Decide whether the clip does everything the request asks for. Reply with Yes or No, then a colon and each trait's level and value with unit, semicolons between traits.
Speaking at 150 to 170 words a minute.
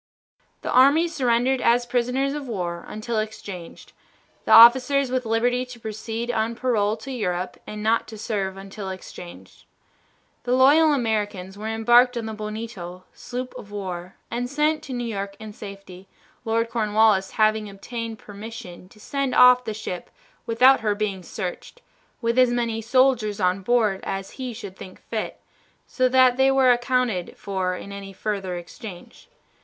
Yes: average, 160 wpm